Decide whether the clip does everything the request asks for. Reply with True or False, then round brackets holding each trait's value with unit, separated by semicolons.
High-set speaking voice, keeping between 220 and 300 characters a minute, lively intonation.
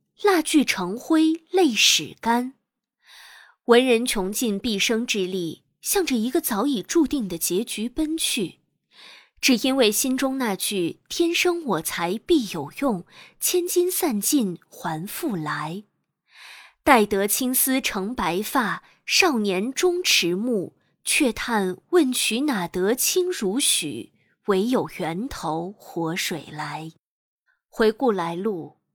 False (235 Hz; 170 characters per minute; 7.2 semitones)